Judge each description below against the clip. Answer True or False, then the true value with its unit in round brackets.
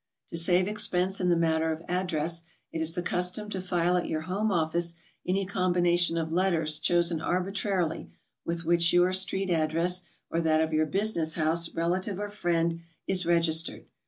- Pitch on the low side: False (175 Hz)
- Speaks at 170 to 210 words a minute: True (175 wpm)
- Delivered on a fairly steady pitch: True (2.0 semitones)